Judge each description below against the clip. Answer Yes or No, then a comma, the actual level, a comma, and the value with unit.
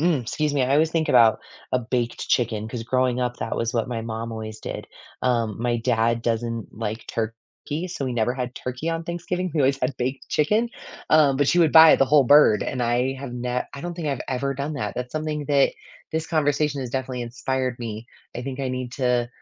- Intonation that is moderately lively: Yes, average, 3.6 semitones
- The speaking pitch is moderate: No, low, 130 Hz